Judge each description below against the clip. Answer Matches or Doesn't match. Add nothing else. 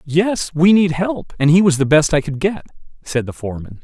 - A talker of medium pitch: Matches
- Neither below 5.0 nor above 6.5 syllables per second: Matches